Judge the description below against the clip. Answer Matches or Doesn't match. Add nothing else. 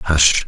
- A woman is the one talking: Doesn't match